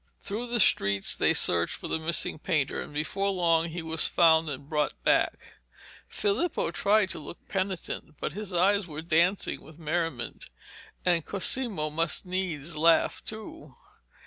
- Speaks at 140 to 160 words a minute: Yes, average, 150 wpm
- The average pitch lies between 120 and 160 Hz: No, medium, 170 Hz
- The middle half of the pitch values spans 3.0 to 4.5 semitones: Yes, average, 4.0 semitones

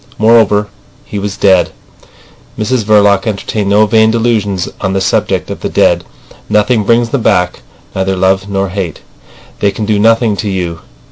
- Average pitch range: No, narrow, 2.3 semitones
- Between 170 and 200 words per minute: No, average, 160 wpm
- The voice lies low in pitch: Yes, low, 105 Hz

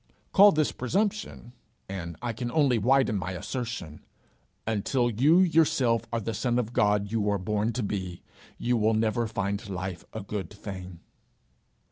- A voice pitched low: Yes, low, 110 Hz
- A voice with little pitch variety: No, average, 3.7 semitones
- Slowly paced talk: No, average, 155 wpm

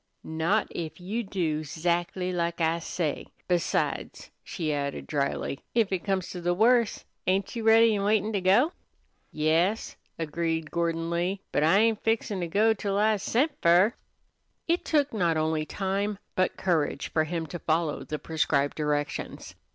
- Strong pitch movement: No, average, 4.3 semitones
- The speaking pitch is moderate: Yes, medium, 175 Hz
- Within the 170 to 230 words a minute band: No, average, 160 wpm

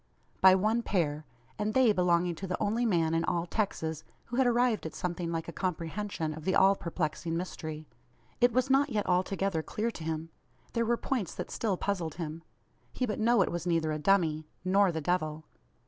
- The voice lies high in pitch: No, medium, 180 Hz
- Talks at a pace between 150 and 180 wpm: No, average, 195 wpm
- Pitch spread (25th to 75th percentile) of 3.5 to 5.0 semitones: Yes, average, 4.7 semitones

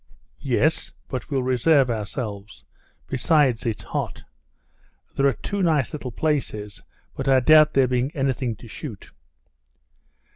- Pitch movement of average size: Yes, average, 3.8 semitones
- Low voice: Yes, low, 130 Hz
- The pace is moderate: No, slow, 125 wpm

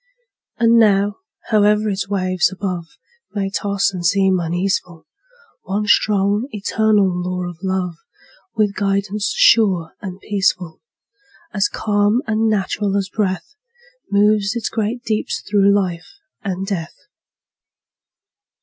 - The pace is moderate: No, slow, 115 wpm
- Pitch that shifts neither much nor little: No, narrow, 2.1 semitones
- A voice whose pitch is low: No, high, 200 Hz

